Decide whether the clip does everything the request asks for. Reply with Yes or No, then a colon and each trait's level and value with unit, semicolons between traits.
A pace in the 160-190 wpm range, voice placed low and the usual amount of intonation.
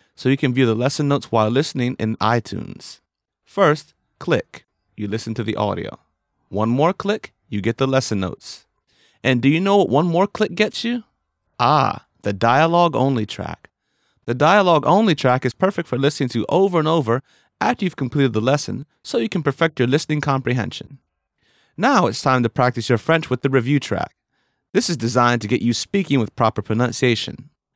No: average, 185 wpm; low, 130 Hz; wide, 5.7 semitones